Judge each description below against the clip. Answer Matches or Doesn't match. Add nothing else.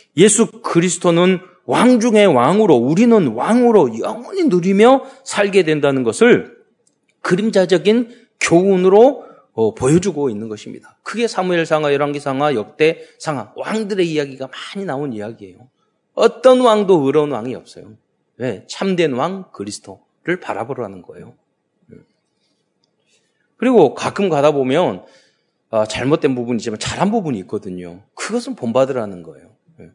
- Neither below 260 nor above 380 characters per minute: Matches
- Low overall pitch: Doesn't match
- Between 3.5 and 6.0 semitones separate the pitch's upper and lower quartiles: Doesn't match